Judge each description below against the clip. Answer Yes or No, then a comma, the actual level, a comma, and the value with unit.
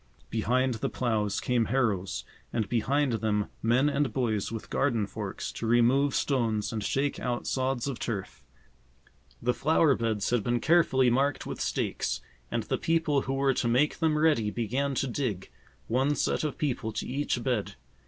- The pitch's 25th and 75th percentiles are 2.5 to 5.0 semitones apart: Yes, average, 3.6 semitones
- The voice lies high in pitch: No, low, 125 Hz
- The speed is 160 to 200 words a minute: Yes, average, 170 wpm